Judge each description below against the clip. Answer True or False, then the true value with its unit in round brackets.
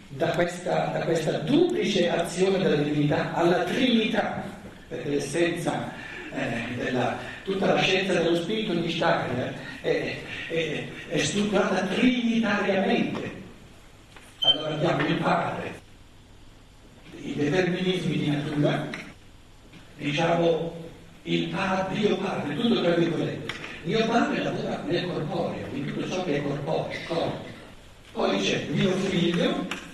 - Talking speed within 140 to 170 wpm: False (120 wpm)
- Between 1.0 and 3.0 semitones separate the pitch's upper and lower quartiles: False (4.3 semitones)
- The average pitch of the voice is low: False (170 Hz)